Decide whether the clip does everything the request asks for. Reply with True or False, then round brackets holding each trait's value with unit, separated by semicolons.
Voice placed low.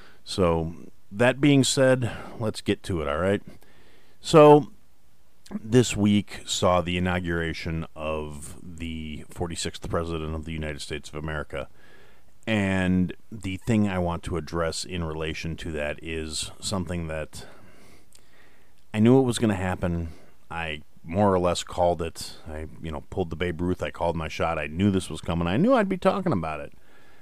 True (85 Hz)